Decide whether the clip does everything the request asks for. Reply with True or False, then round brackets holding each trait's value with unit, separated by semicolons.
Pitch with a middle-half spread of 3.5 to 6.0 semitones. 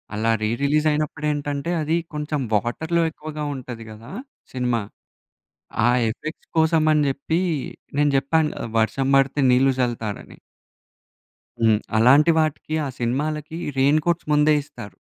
True (3.9 semitones)